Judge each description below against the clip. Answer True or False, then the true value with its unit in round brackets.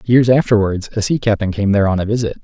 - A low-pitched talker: True (105 Hz)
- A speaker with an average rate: False (245 wpm)